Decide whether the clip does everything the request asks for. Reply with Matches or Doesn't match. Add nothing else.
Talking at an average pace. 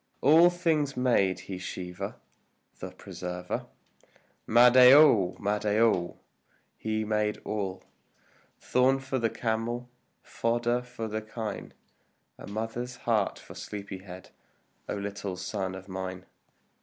Doesn't match